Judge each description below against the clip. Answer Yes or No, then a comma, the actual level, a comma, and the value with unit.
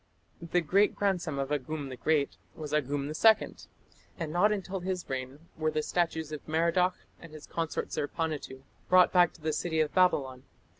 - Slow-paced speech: No, average, 170 wpm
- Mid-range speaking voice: Yes, medium, 160 Hz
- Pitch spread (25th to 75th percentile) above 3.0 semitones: Yes, average, 3.4 semitones